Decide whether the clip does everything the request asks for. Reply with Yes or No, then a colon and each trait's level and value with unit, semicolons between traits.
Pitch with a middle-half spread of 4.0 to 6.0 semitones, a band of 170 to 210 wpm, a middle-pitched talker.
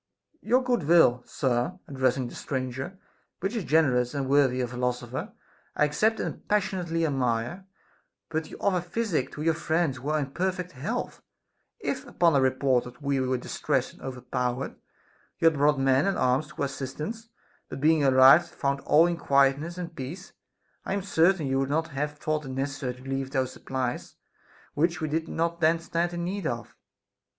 Yes: average, 4.4 semitones; average, 180 wpm; medium, 145 Hz